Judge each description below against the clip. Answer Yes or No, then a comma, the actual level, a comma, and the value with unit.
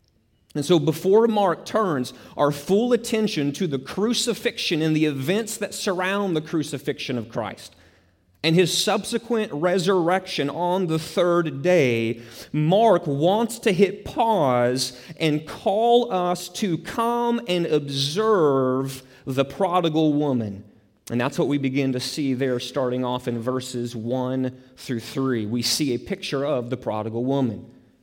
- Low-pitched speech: No, medium, 150 Hz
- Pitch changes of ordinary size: No, wide, 6.9 semitones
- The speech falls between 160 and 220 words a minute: No, average, 140 wpm